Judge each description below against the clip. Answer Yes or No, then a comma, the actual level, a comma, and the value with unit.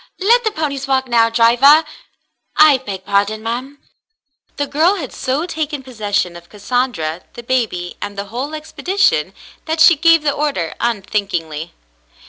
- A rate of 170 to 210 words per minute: No, average, 145 wpm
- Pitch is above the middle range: Yes, very high, 255 Hz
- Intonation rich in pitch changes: Yes, wide, 6.9 semitones